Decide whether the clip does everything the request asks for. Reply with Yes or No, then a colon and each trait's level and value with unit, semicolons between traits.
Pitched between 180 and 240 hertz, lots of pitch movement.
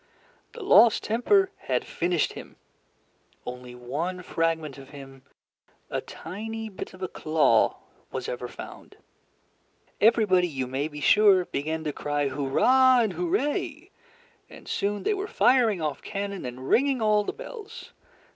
Yes: medium, 185 Hz; wide, 8.5 semitones